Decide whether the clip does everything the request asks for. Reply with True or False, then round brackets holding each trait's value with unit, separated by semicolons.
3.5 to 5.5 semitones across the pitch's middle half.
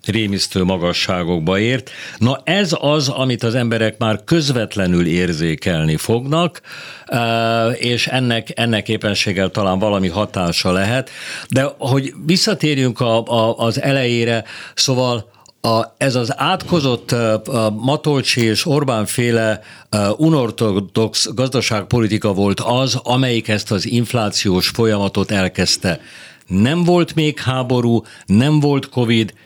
True (4.0 semitones)